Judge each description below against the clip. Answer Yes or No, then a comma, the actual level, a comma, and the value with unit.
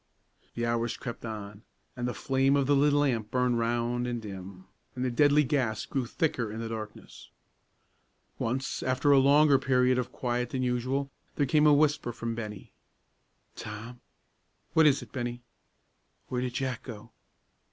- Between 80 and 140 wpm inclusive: No, average, 165 wpm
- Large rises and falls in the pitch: No, average, 2.8 semitones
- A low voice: Yes, low, 125 Hz